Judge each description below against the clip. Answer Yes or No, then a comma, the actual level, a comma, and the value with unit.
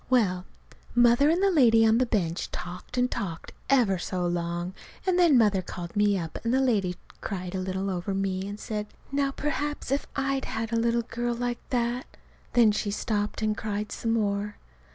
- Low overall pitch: No, high, 215 Hz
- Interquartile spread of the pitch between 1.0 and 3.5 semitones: No, average, 4.4 semitones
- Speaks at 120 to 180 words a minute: No, average, 195 wpm